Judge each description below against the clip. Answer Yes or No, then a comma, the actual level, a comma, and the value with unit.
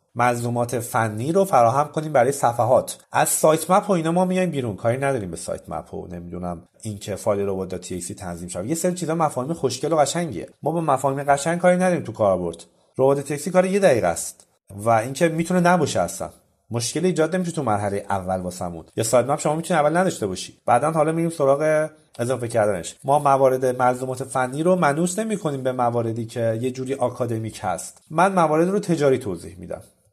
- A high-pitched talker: No, low, 135 Hz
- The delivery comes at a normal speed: No, fast, 190 wpm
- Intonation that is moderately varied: No, wide, 6.2 semitones